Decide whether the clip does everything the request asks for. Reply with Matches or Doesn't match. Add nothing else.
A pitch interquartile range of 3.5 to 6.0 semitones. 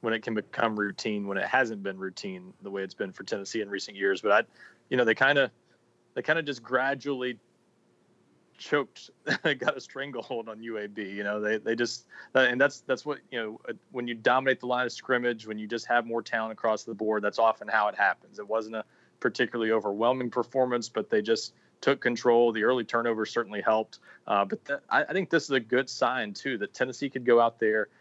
Doesn't match